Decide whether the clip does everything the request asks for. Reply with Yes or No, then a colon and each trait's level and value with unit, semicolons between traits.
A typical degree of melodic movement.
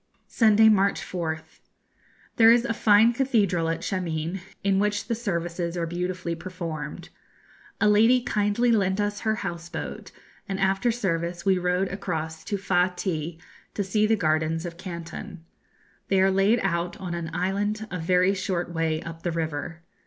Yes: average, 3.4 semitones